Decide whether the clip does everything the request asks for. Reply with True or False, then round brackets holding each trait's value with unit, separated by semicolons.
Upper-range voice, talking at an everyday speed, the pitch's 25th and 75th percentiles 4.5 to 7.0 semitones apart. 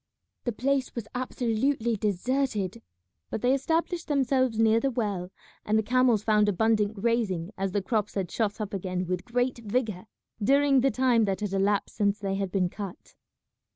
False (220 Hz; 170 wpm; 4.1 semitones)